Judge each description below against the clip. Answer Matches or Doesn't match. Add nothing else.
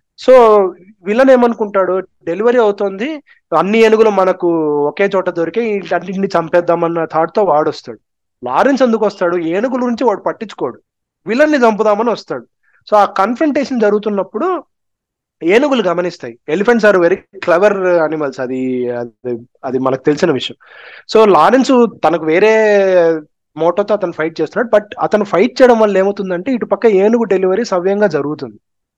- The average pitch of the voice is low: Doesn't match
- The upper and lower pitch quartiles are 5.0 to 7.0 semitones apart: Matches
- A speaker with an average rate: Doesn't match